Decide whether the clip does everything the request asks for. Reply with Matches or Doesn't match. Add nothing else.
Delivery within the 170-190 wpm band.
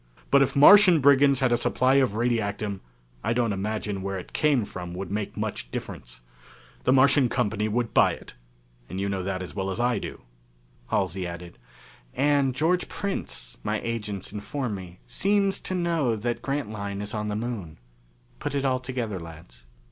Matches